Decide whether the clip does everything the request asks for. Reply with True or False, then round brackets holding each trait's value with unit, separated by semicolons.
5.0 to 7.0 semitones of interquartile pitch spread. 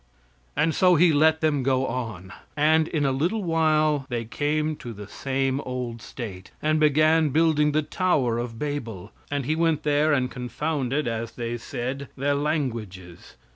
False (4.4 semitones)